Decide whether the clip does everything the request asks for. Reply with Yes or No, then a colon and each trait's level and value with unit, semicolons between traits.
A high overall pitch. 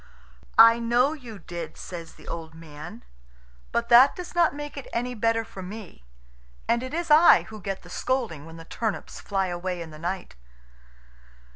Yes: high, 215 Hz